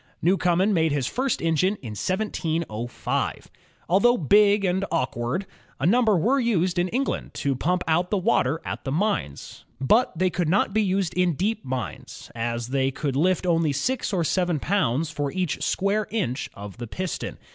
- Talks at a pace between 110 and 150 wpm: No, average, 170 wpm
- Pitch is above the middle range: No, medium, 175 Hz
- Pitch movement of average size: No, wide, 6.0 semitones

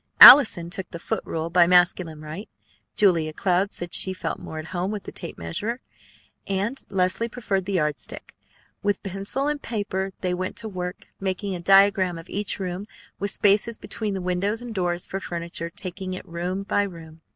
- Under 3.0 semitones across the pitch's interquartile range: Yes, narrow, 2.6 semitones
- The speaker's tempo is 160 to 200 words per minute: Yes, average, 180 wpm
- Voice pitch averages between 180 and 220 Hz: Yes, medium, 185 Hz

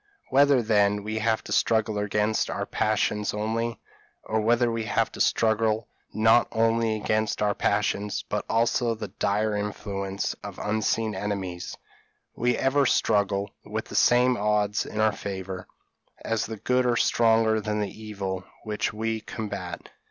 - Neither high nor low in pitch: No, low, 110 Hz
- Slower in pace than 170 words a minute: Yes, average, 150 wpm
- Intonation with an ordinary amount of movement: No, narrow, 1.7 semitones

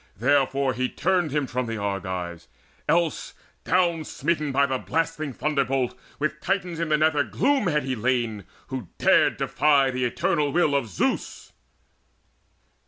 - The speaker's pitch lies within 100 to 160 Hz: Yes, medium, 140 Hz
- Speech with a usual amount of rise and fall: Yes, average, 3.8 semitones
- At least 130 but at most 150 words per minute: Yes, average, 145 wpm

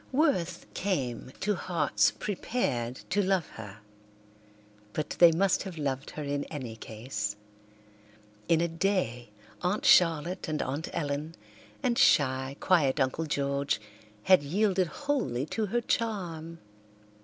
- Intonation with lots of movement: Yes, wide, 6.0 semitones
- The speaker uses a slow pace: Yes, slow, 125 wpm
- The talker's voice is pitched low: No, medium, 160 Hz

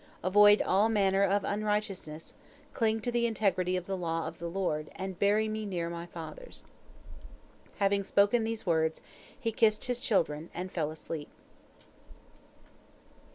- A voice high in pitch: Yes, high, 195 Hz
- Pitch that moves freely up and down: No, average, 4.0 semitones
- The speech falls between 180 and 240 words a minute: No, average, 145 wpm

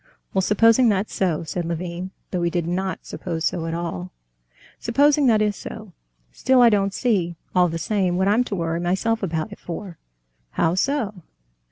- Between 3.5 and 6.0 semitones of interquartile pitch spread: Yes, average, 4.0 semitones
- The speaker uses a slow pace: No, average, 180 wpm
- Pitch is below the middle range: No, high, 190 Hz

